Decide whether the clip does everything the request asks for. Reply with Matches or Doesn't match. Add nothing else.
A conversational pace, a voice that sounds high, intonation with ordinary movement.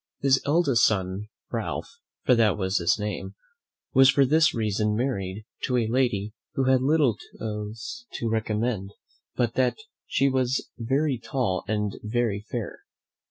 Doesn't match